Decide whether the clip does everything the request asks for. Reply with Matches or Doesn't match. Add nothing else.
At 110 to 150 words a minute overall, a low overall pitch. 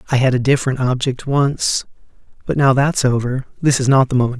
Doesn't match